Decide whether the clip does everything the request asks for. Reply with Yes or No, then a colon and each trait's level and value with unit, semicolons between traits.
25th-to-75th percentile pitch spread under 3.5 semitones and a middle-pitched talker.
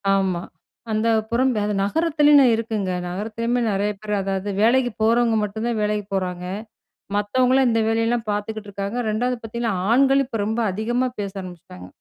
No: average, 3.0 semitones; high, 220 Hz